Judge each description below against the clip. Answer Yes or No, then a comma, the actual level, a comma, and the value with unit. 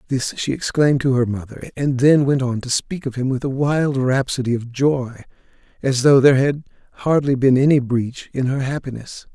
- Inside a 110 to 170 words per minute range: No, average, 200 wpm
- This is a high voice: No, low, 130 Hz